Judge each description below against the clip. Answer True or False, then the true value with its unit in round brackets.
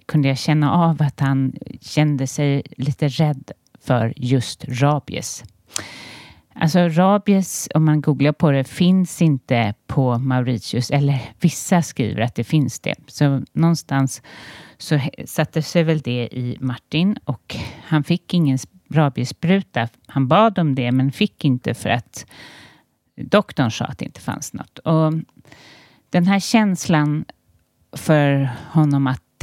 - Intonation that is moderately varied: True (3.8 semitones)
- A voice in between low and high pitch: True (145 Hz)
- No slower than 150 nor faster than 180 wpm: False (140 wpm)